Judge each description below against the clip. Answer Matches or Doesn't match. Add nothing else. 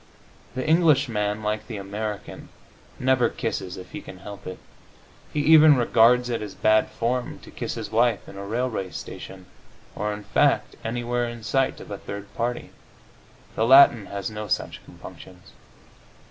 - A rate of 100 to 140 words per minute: Doesn't match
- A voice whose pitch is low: Matches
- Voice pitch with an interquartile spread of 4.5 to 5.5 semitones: Doesn't match